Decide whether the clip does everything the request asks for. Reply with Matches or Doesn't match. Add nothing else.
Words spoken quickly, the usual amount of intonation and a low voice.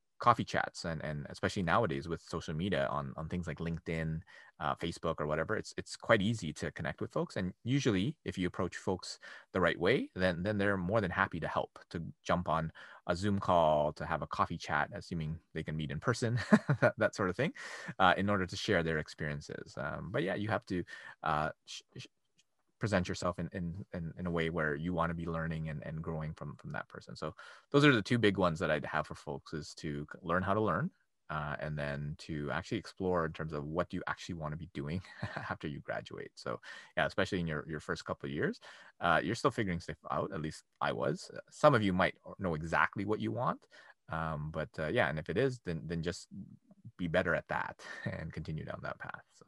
Matches